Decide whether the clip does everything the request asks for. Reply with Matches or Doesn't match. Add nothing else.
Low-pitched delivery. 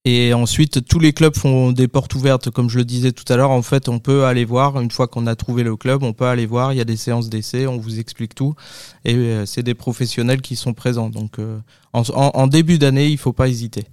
Matches